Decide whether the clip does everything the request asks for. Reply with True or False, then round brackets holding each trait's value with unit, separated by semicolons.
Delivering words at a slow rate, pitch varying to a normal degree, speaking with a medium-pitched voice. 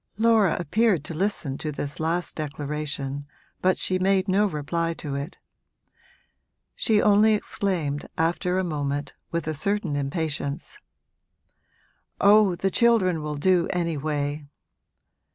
True (120 wpm; 4.8 semitones; 165 Hz)